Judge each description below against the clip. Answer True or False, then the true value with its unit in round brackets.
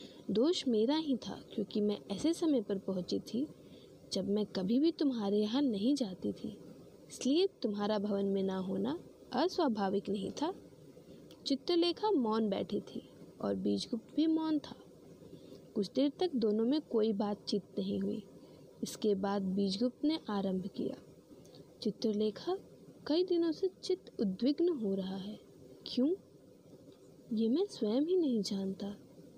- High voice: True (225 Hz)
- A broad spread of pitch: True (6.9 semitones)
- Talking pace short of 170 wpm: True (140 wpm)